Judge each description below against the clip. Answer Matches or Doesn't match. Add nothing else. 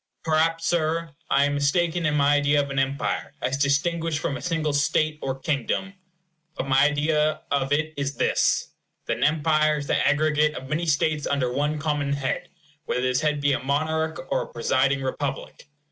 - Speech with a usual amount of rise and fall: Doesn't match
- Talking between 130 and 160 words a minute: Doesn't match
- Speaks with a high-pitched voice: Doesn't match